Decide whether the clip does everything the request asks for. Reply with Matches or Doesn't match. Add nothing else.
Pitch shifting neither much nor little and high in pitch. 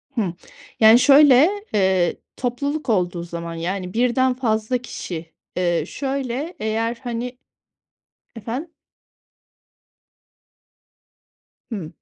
Doesn't match